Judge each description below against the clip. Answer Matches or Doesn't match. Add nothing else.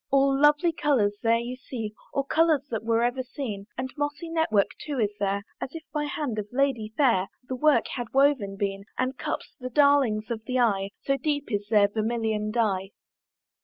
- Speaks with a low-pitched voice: Doesn't match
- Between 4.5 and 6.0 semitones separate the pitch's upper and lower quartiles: Matches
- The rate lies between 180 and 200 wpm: Matches